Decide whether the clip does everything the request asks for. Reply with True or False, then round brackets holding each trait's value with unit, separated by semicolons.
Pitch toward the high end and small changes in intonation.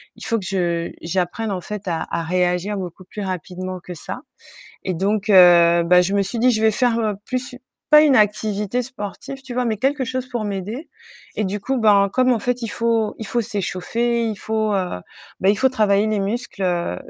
False (210 Hz; 4.0 semitones)